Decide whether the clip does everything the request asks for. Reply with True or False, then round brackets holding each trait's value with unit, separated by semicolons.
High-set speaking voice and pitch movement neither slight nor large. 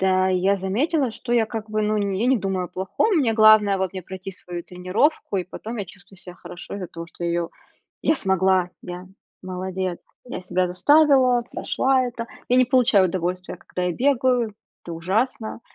True (195 Hz; 4.6 semitones)